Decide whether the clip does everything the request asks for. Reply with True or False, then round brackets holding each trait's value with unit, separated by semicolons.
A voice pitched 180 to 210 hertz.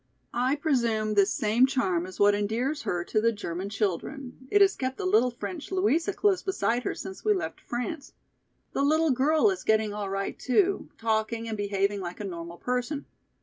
False (240 Hz)